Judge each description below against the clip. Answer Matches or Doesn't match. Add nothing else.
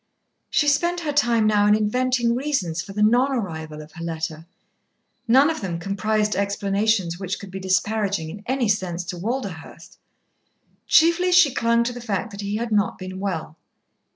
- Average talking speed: Matches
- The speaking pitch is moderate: Doesn't match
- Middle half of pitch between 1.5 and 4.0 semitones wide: Doesn't match